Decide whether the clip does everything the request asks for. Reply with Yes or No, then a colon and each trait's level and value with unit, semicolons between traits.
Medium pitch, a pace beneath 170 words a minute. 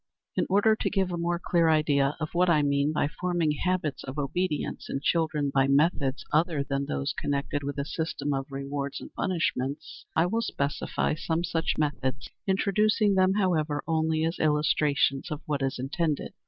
No: medium, 155 Hz; average, 175 wpm